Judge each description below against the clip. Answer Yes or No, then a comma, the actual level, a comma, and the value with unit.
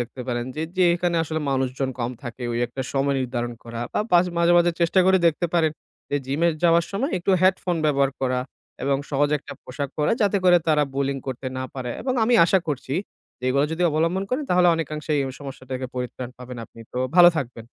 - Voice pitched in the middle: Yes, medium, 145 Hz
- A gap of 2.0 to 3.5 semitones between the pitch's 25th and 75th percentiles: No, average, 4.9 semitones